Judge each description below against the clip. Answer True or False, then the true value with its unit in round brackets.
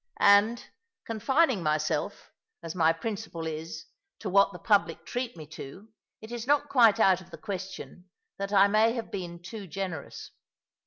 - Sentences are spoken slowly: False (160 wpm)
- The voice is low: False (200 Hz)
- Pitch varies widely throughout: False (4.7 semitones)